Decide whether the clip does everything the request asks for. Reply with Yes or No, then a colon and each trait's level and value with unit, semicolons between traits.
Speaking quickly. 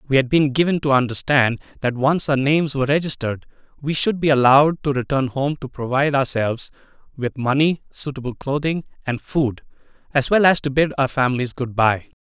No: average, 180 wpm